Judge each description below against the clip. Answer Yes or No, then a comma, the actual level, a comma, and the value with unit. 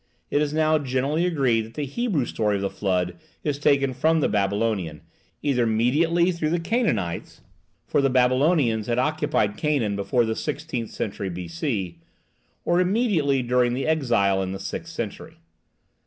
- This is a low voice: Yes, low, 130 Hz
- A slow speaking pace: No, average, 155 wpm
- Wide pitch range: Yes, wide, 6.8 semitones